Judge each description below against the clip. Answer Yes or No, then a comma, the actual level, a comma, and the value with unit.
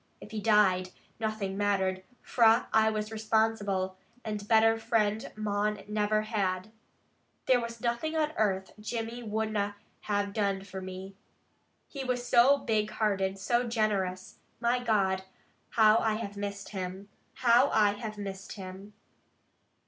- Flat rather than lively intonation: Yes, narrow, 2.3 semitones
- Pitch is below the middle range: No, high, 210 Hz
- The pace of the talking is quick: No, average, 140 wpm